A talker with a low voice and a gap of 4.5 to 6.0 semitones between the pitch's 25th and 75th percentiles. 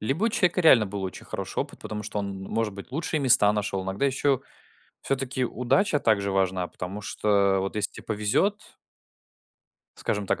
Yes: low, 105 Hz; wide, 5.4 semitones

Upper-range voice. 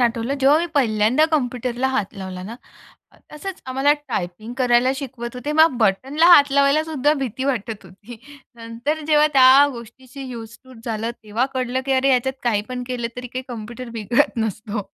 Yes: very high, 250 Hz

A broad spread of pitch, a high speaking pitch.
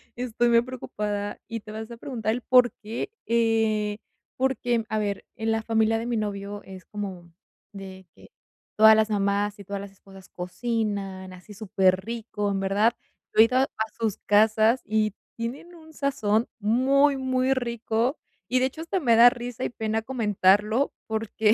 No: average, 2.8 semitones; high, 220 Hz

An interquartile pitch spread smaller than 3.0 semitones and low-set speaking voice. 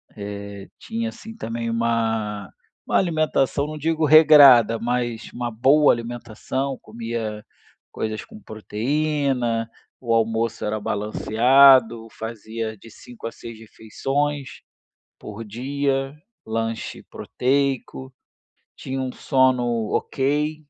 No: average, 3.8 semitones; low, 120 Hz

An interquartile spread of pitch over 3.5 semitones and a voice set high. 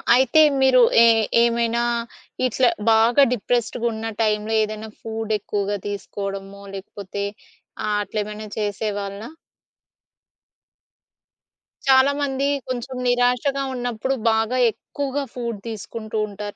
No: average, 3.0 semitones; high, 225 Hz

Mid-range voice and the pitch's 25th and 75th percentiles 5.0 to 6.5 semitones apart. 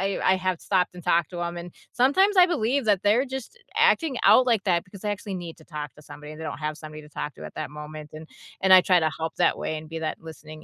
Yes: medium, 175 Hz; wide, 5.6 semitones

